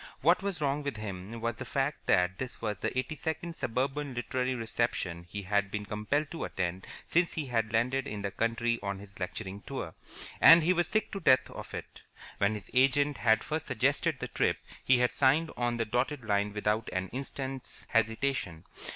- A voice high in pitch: No, low, 120 Hz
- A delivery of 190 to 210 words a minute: Yes, average, 195 wpm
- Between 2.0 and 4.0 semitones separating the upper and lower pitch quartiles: No, average, 5.0 semitones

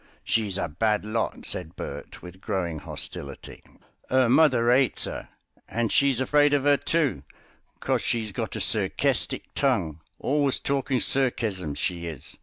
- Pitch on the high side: No, low, 115 Hz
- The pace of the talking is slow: No, average, 145 wpm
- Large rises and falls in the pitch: Yes, wide, 6.9 semitones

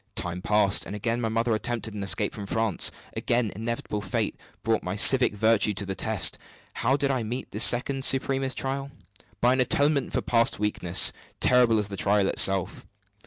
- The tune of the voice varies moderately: Yes, average, 3.6 semitones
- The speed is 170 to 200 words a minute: Yes, average, 180 wpm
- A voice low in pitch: Yes, low, 115 Hz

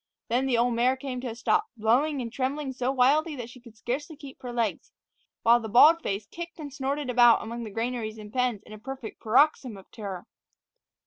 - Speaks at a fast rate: Yes, fast, 210 wpm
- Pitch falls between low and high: No, high, 245 Hz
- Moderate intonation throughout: Yes, average, 3.0 semitones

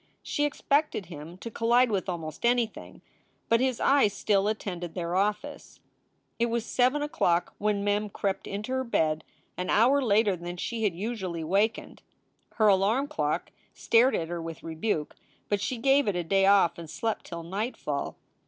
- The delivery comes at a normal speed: Yes, average, 170 wpm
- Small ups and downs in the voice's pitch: No, average, 5.2 semitones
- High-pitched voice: Yes, high, 205 Hz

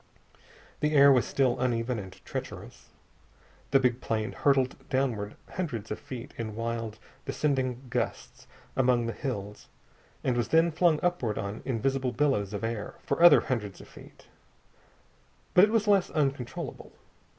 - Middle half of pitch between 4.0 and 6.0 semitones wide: No, average, 3.6 semitones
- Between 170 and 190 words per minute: No, average, 145 wpm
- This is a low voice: Yes, low, 125 Hz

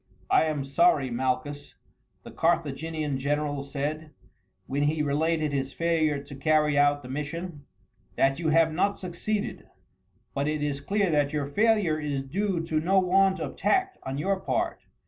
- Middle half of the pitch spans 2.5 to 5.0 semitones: Yes, average, 3.3 semitones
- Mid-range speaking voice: Yes, medium, 155 Hz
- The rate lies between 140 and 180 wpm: Yes, average, 160 wpm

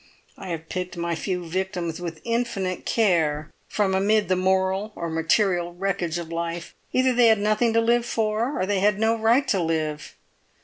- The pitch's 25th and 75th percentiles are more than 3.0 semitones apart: Yes, average, 4.1 semitones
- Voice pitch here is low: No, high, 190 Hz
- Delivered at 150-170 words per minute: No, average, 180 wpm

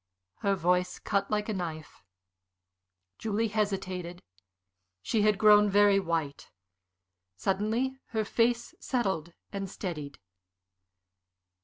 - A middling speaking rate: No, slow, 100 wpm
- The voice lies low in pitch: No, high, 200 Hz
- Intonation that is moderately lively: Yes, average, 3.1 semitones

